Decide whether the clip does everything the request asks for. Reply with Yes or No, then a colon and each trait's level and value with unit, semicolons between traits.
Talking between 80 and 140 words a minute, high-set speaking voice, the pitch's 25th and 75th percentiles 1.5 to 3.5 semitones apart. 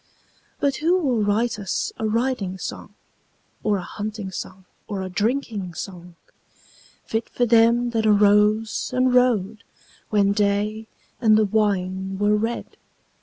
Yes: slow, 135 wpm; high, 215 Hz; narrow, 2.5 semitones